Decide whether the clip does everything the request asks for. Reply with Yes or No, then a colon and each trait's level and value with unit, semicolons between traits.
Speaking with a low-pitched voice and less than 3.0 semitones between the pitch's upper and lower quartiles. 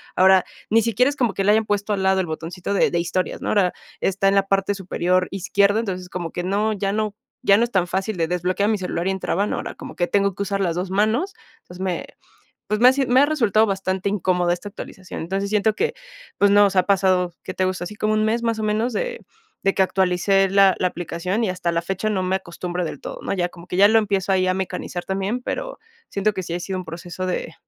No: high, 195 Hz; narrow, 2.5 semitones